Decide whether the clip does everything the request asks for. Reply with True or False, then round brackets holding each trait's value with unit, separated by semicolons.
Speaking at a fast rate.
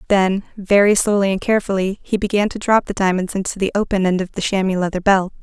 True (220 wpm)